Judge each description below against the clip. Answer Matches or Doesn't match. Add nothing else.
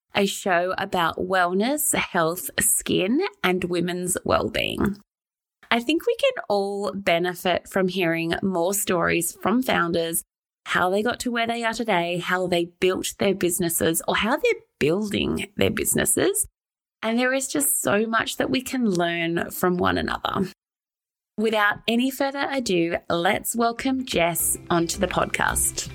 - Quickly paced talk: Doesn't match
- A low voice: Doesn't match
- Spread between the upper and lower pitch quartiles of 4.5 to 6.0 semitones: Matches